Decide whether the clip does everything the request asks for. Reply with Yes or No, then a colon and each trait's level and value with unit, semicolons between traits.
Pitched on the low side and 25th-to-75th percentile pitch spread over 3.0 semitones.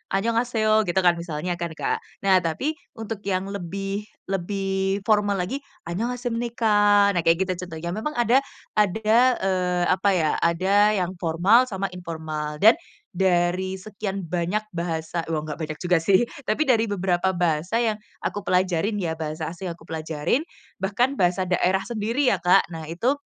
No: high, 190 Hz; average, 3.7 semitones